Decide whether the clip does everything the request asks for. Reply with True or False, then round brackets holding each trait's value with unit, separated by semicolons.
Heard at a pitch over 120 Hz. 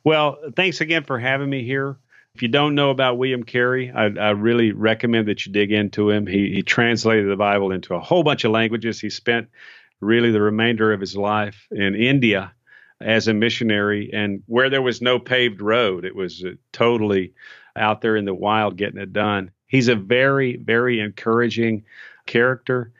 False (115 Hz)